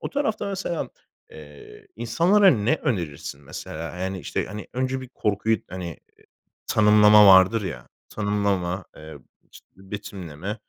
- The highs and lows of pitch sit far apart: No, average, 4.4 semitones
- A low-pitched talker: Yes, low, 100 Hz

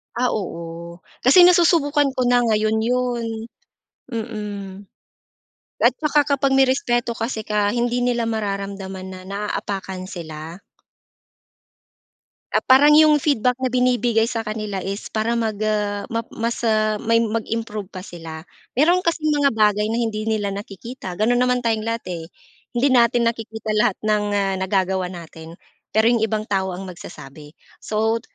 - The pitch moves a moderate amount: Yes, average, 3.6 semitones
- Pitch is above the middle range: Yes, high, 220 Hz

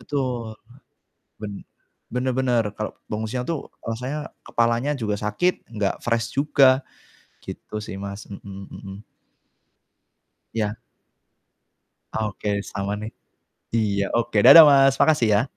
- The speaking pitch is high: No, low, 115 Hz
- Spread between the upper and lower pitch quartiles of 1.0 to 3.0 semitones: No, average, 3.8 semitones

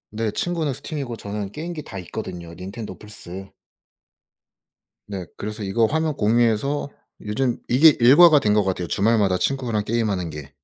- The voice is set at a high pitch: No, low, 110 Hz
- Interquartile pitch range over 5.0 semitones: Yes, wide, 5.6 semitones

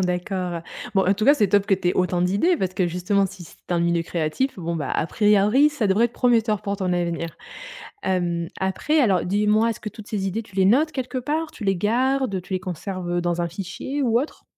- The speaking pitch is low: No, high, 195 Hz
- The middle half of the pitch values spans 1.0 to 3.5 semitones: No, average, 4.2 semitones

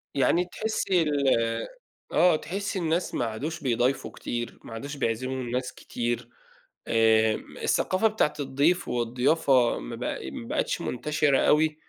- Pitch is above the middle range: No, low, 135 Hz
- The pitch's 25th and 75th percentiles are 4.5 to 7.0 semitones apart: Yes, average, 5.1 semitones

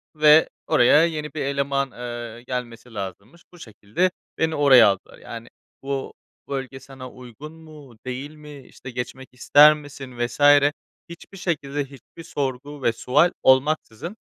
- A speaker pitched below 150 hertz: Yes, low, 135 Hz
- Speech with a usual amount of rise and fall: Yes, average, 3.5 semitones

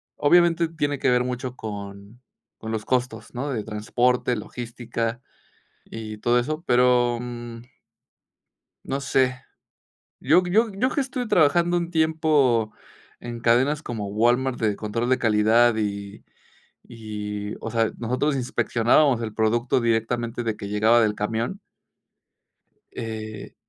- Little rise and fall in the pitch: No, average, 3.2 semitones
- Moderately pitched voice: No, low, 120 Hz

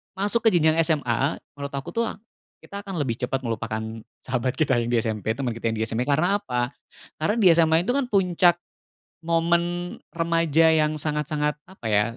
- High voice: No, medium, 155 Hz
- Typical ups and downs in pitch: No, wide, 5.9 semitones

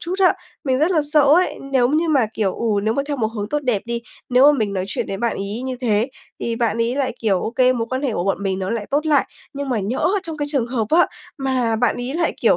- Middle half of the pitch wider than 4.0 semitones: Yes, average, 4.4 semitones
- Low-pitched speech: No, very high, 250 Hz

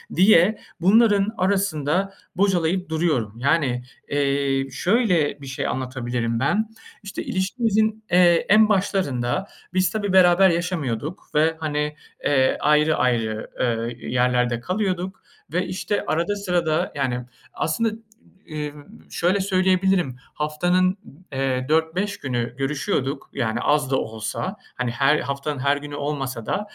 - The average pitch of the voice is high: No, medium, 155 Hz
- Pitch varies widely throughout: Yes, wide, 5.9 semitones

